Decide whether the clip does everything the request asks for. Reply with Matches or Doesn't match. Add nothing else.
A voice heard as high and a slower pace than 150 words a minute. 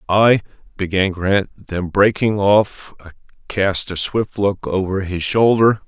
Doesn't match